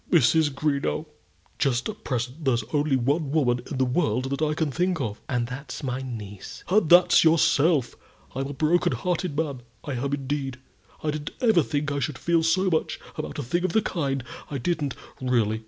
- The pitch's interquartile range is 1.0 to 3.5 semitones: No, average, 3.9 semitones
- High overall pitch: No, medium, 145 Hz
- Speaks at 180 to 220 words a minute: Yes, average, 190 wpm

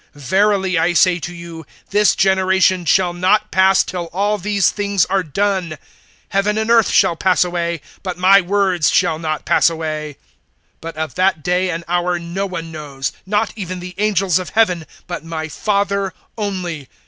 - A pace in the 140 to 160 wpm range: No, average, 170 wpm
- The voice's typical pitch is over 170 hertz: Yes, medium, 185 Hz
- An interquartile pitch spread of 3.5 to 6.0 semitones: No, average, 2.8 semitones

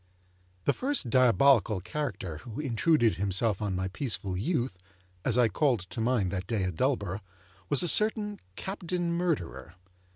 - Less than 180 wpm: Yes, average, 150 wpm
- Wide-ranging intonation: Yes, wide, 8.1 semitones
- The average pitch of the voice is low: Yes, low, 115 Hz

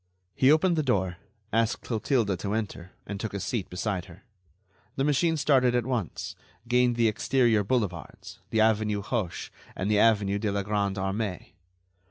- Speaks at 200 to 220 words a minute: No, average, 165 wpm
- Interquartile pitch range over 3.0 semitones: Yes, average, 3.7 semitones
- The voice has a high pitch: No, low, 110 Hz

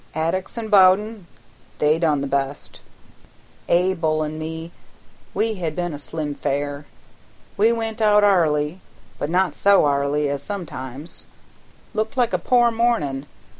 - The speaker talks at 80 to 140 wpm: Yes, slow, 135 wpm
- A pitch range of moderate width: No, wide, 5.8 semitones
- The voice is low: No, medium, 165 Hz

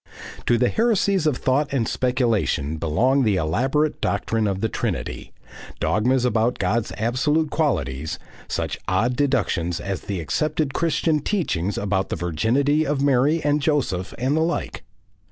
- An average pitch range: No, wide, 7.0 semitones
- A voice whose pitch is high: No, low, 125 Hz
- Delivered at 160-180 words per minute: No, average, 145 wpm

